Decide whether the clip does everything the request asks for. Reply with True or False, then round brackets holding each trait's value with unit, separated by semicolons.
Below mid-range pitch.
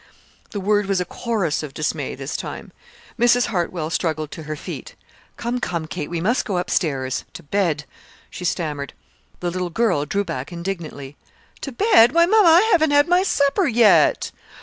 False (185 Hz)